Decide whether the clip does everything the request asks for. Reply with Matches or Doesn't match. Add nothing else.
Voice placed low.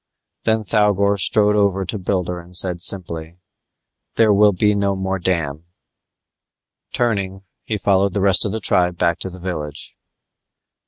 Matches